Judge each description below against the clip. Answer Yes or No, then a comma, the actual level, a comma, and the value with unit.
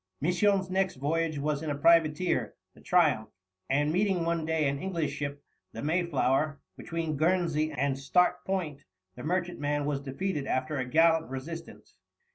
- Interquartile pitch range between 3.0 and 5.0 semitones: Yes, average, 3.4 semitones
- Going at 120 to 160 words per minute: Yes, average, 150 wpm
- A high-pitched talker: No, medium, 155 Hz